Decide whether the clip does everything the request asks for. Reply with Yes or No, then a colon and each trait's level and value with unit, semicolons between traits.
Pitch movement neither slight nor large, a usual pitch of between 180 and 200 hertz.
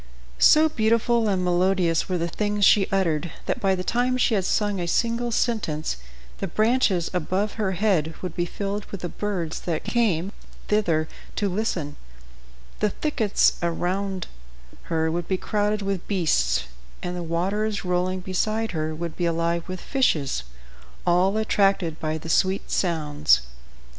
Yes: average, 3.8 semitones; medium, 185 Hz